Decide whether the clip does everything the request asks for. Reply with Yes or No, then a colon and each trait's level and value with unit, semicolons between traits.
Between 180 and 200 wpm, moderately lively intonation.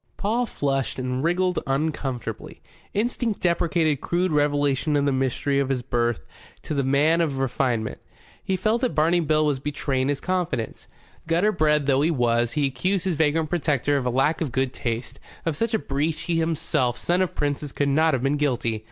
Yes: average, 185 wpm; average, 3.8 semitones